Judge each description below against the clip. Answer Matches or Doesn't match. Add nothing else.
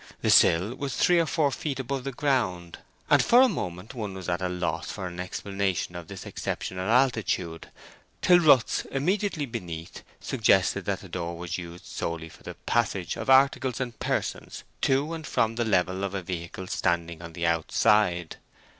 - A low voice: Matches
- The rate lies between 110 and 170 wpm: Doesn't match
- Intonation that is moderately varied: Doesn't match